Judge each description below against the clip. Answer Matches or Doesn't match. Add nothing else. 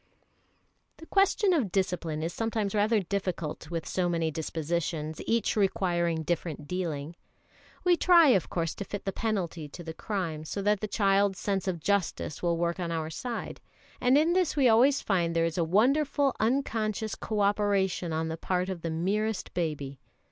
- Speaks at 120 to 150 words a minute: Doesn't match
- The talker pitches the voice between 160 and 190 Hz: Matches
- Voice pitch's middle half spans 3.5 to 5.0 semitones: Matches